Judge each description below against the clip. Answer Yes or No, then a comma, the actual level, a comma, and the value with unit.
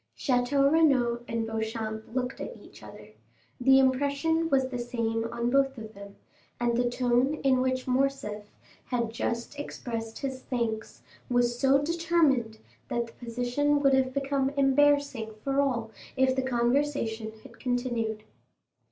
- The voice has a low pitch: No, very high, 250 Hz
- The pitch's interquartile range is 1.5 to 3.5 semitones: Yes, average, 2.9 semitones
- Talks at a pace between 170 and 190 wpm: No, average, 145 wpm